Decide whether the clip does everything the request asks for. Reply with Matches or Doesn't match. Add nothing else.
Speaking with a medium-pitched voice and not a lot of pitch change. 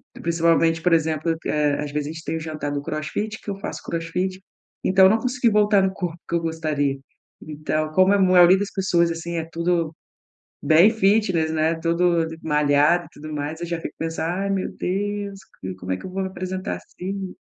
Doesn't match